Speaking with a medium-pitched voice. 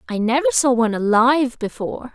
No: high, 245 Hz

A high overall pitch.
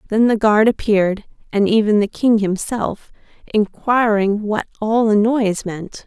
Yes: high, 215 Hz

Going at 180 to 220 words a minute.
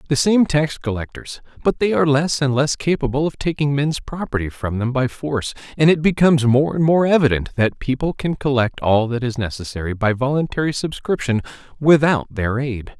Yes: average, 185 wpm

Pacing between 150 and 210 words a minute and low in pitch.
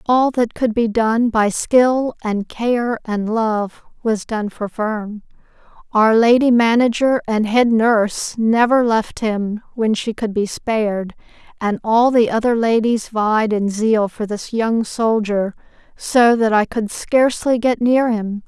No: average, 160 wpm; high, 225 Hz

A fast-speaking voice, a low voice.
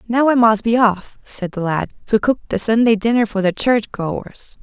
No: fast, 220 wpm; high, 220 Hz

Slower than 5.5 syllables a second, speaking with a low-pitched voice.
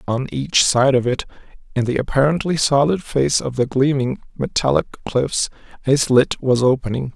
Yes: 4.6 syllables/s; low, 130 Hz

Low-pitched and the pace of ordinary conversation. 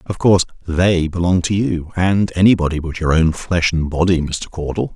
Yes: very low, 85 Hz; average, 195 wpm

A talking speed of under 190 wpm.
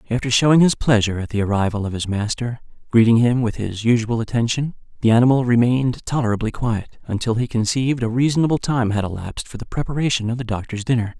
No: average, 195 wpm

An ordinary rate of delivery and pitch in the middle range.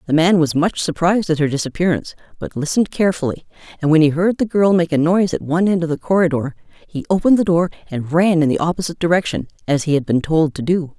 No: fast, 235 wpm; medium, 165 Hz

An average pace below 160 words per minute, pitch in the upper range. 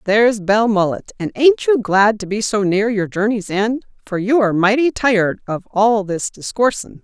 No: average, 180 wpm; high, 215 Hz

